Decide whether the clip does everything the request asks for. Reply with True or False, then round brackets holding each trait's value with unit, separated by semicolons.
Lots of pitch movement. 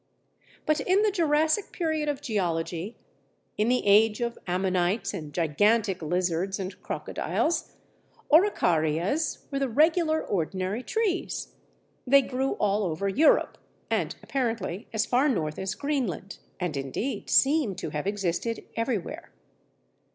True (7.6 semitones)